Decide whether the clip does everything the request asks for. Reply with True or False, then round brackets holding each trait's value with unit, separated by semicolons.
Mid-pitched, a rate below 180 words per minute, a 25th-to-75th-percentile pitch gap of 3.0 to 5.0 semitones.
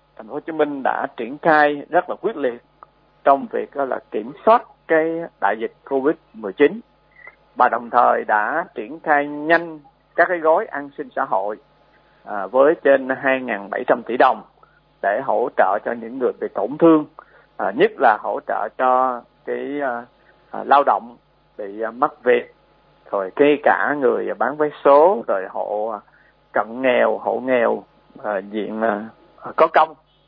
True (145 Hz; 165 wpm; 4.4 semitones)